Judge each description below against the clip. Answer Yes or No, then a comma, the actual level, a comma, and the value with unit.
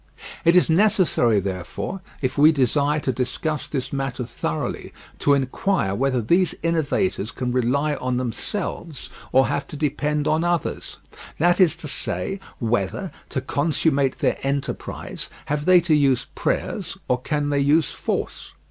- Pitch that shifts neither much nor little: Yes, average, 4.0 semitones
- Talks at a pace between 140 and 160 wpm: Yes, average, 150 wpm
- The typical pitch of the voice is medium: Yes, medium, 145 Hz